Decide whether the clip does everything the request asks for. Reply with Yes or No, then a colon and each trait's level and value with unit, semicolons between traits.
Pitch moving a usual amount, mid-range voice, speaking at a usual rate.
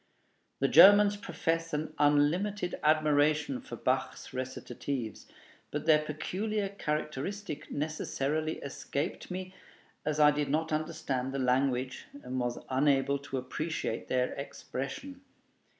No: average, 3.3 semitones; medium, 150 Hz; slow, 115 wpm